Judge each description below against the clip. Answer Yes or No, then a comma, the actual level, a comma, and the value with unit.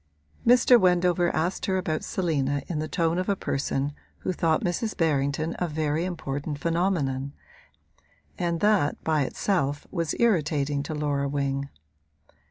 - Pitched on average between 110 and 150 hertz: No, medium, 160 Hz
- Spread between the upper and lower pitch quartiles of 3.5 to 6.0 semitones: Yes, average, 3.9 semitones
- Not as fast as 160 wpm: Yes, average, 140 wpm